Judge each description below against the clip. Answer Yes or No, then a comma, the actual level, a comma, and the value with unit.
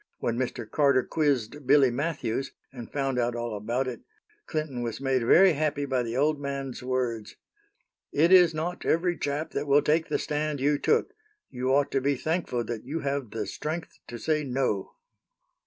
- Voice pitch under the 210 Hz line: Yes, medium, 140 Hz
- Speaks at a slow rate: No, average, 180 wpm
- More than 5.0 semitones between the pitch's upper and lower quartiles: No, average, 3.6 semitones